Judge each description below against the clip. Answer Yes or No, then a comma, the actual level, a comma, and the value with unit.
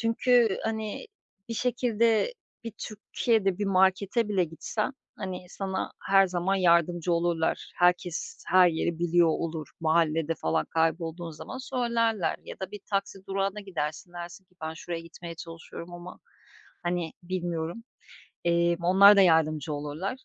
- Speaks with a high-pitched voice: No, medium, 175 Hz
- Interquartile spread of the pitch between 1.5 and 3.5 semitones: Yes, average, 3.2 semitones